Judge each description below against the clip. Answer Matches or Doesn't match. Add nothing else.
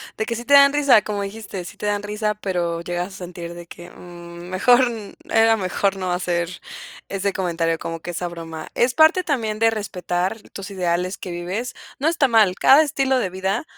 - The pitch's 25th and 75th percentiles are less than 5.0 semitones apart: Matches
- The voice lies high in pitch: Matches